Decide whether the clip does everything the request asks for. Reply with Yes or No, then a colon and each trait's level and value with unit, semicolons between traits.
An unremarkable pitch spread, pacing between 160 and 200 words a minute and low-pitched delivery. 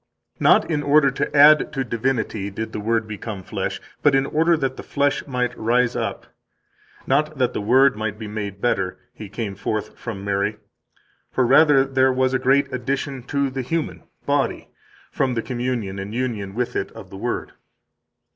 Yes: average, 4.3 semitones; average, 180 wpm; low, 125 Hz